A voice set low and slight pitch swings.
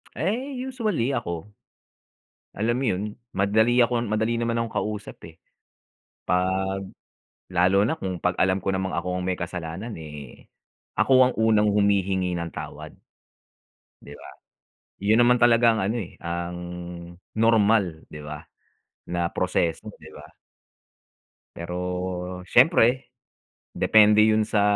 No: low, 100 Hz; average, 4.3 semitones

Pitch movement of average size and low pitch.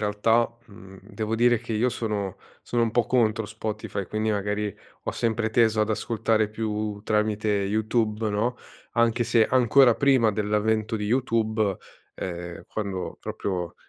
No: narrow, 1.8 semitones; low, 110 Hz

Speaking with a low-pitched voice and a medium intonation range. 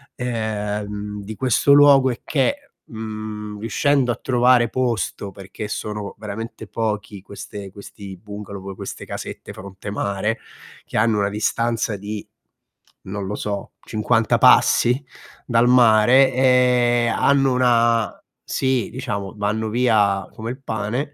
Yes: low, 110 Hz; average, 3.2 semitones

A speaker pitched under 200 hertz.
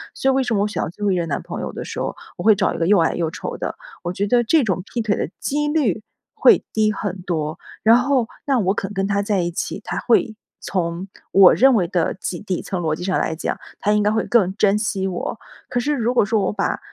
No: high, 205 Hz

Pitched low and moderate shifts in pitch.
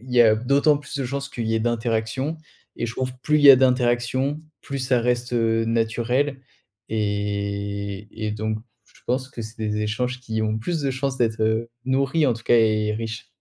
Yes: low, 120 Hz; average, 3.0 semitones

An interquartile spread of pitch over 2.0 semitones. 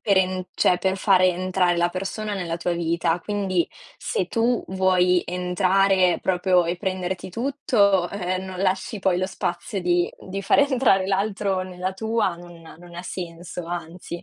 No: narrow, 1.7 semitones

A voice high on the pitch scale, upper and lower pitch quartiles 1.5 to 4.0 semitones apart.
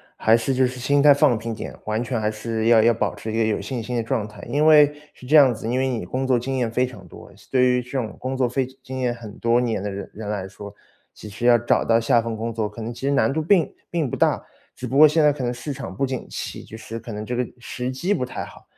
No: low, 120 Hz; average, 3.0 semitones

